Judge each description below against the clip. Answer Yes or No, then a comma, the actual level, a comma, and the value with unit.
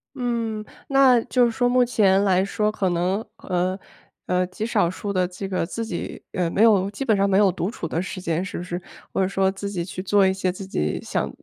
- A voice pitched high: Yes, high, 195 Hz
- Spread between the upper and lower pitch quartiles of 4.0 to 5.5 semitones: No, average, 3.0 semitones